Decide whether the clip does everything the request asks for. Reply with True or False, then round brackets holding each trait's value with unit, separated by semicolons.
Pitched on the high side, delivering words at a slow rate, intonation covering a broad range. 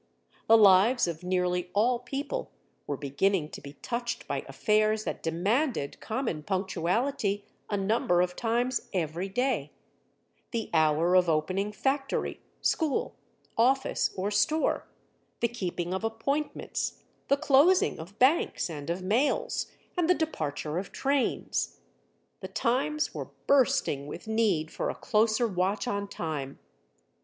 True (210 Hz; 130 wpm; 6.1 semitones)